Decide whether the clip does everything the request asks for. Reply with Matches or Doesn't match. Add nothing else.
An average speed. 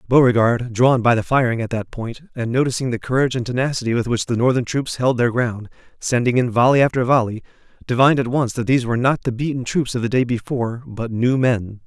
Doesn't match